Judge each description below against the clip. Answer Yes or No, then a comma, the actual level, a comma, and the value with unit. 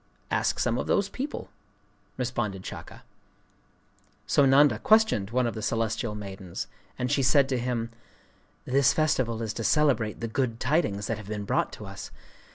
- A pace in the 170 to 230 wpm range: No, average, 160 wpm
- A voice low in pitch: Yes, low, 120 Hz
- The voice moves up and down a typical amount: Yes, average, 4.1 semitones